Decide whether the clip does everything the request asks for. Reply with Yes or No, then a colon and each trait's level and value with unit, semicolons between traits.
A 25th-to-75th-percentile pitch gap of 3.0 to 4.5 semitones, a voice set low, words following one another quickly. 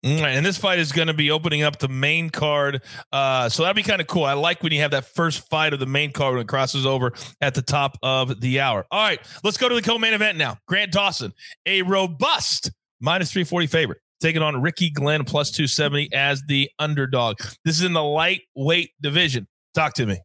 No: average, 3.6 semitones; medium, 150 Hz; fast, 230 wpm